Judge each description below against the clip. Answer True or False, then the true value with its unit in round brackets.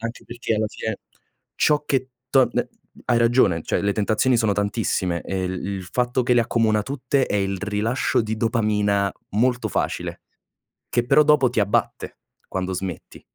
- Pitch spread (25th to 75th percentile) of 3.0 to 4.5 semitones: True (3.4 semitones)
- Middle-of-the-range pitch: False (110 Hz)